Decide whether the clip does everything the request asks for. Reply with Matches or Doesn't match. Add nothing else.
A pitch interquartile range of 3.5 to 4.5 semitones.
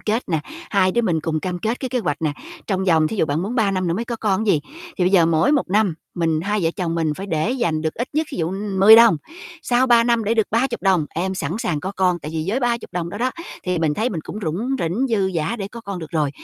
Doesn't match